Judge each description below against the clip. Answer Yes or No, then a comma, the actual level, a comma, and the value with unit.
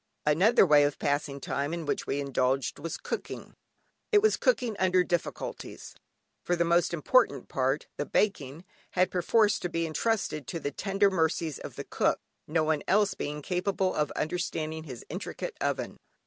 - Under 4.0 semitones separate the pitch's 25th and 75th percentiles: No, average, 4.3 semitones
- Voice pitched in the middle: Yes, medium, 165 Hz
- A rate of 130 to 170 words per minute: Yes, average, 165 wpm